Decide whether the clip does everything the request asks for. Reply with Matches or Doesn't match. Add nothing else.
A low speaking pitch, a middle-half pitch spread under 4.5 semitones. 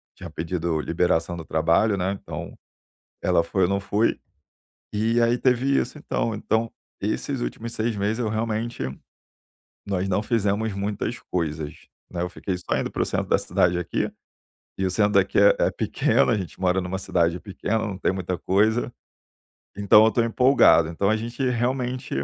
Matches